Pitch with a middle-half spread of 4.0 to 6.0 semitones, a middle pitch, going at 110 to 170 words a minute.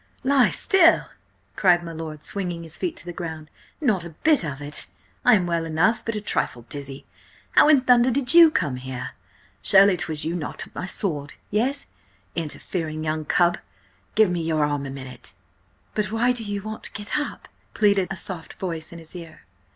No: wide, 5.6 semitones; medium, 175 Hz; average, 190 wpm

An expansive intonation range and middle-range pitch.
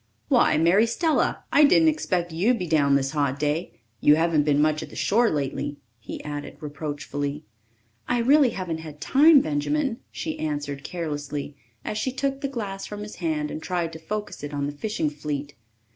Yes: wide, 6.6 semitones; medium, 160 Hz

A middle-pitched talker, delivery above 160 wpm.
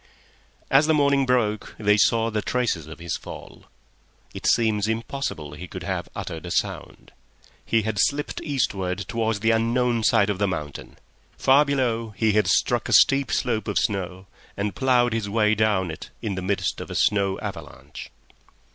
No: low, 110 Hz; average, 175 wpm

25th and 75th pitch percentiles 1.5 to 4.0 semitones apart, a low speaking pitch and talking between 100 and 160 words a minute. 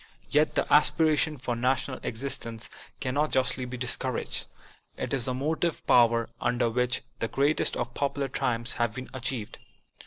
Yes: average, 3.0 semitones; low, 130 Hz; average, 155 wpm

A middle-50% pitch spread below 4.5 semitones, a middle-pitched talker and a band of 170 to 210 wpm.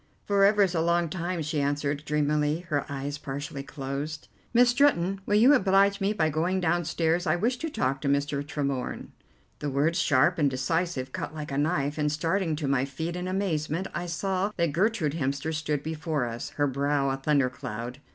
Yes: average, 4.0 semitones; medium, 155 Hz; average, 190 wpm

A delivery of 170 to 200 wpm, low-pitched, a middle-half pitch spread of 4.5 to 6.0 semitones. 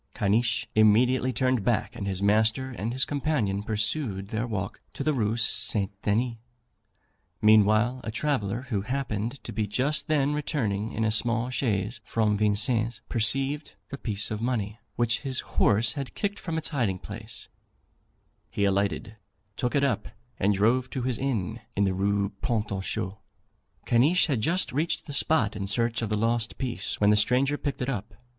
No: average, 175 wpm; low, 115 Hz; average, 3.8 semitones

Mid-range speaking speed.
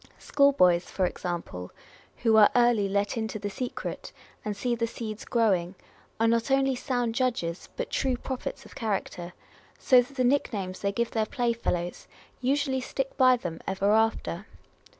Yes: average, 165 wpm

